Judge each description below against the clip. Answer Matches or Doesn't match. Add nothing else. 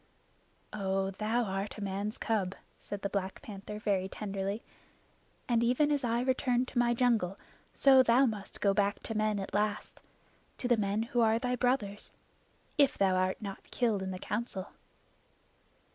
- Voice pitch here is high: Matches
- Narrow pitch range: Doesn't match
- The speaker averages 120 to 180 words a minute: Matches